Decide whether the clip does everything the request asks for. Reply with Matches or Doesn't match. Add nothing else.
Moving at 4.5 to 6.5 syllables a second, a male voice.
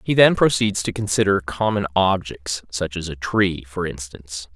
Matches